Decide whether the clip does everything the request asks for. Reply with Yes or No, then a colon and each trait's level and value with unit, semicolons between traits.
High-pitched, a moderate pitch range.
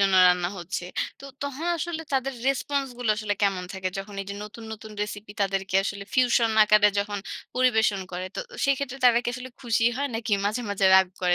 Yes: high, 215 Hz; average, 4.5 semitones